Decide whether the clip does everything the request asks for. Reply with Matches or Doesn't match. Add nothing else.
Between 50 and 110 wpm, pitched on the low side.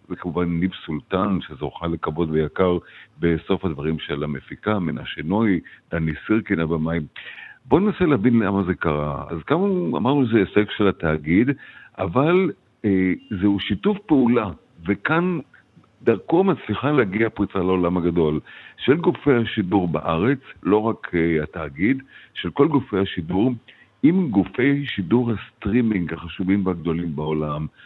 Doesn't match